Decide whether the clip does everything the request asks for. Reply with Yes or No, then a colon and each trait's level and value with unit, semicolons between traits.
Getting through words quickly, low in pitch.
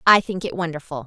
No: fast, 225 wpm; medium, 170 Hz